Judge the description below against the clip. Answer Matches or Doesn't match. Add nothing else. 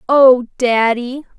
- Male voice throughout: Doesn't match